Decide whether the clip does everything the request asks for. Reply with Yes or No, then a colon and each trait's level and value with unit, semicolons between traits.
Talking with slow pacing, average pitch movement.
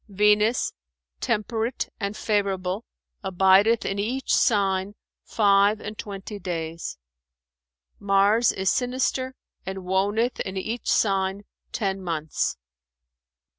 No: slow, 95 wpm; narrow, 2.3 semitones